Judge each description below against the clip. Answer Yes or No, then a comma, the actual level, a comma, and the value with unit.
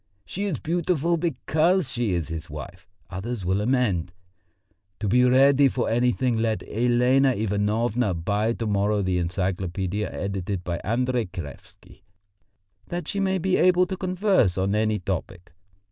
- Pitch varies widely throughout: Yes, wide, 6.2 semitones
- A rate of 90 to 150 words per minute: Yes, average, 145 wpm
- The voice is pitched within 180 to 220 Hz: No, low, 115 Hz